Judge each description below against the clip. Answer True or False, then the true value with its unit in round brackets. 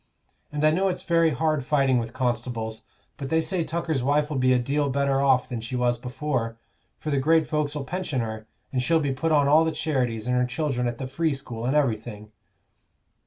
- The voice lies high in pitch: False (135 Hz)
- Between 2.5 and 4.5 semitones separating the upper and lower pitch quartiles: True (3.8 semitones)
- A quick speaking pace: True (210 wpm)